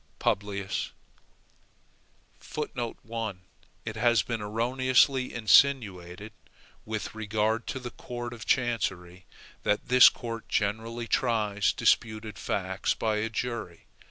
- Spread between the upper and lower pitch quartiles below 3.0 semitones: Yes, narrow, 2.5 semitones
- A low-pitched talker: Yes, low, 110 Hz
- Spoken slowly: Yes, slow, 100 wpm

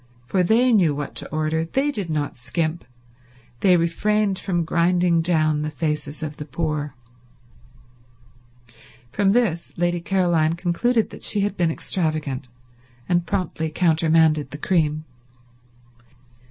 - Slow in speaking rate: Yes, slow, 125 wpm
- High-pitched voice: No, medium, 165 Hz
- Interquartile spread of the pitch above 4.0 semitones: No, average, 3.0 semitones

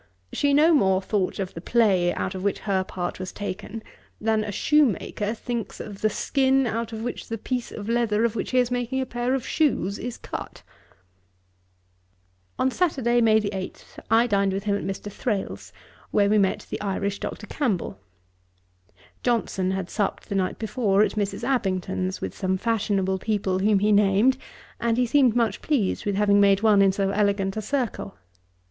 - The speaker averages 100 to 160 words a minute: No, average, 180 wpm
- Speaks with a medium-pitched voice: No, high, 210 Hz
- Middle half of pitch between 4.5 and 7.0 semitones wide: No, average, 3.4 semitones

